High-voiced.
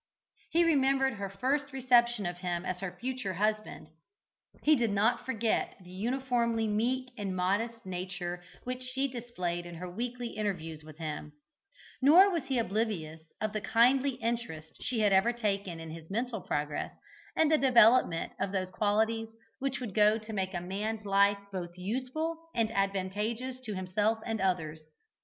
Yes: high, 215 Hz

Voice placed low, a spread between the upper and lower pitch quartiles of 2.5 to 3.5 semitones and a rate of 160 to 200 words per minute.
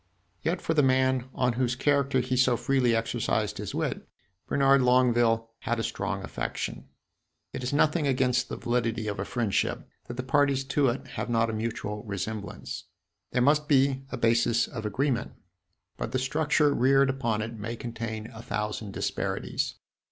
Yes: low, 125 Hz; average, 3.0 semitones; average, 165 wpm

